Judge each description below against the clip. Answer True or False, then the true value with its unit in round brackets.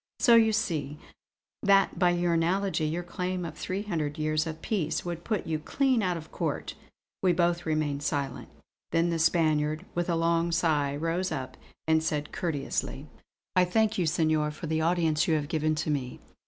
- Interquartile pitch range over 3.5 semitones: False (2.5 semitones)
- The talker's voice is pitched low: False (165 Hz)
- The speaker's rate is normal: True (180 wpm)